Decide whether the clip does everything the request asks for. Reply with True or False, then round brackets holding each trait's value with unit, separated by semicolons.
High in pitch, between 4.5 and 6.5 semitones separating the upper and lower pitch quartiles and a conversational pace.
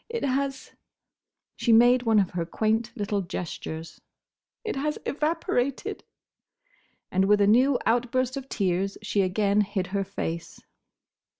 False (215 Hz; 4.8 semitones; 115 wpm)